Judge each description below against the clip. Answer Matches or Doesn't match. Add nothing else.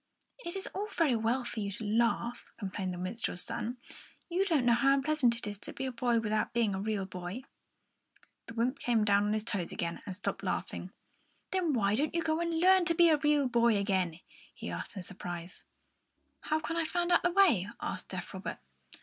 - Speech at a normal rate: Doesn't match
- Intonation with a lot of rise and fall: Matches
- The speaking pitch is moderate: Doesn't match